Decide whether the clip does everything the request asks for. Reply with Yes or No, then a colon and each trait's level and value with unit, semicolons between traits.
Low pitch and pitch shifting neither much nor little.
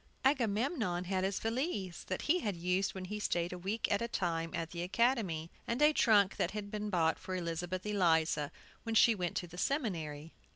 No: high, 190 Hz; average, 4.4 semitones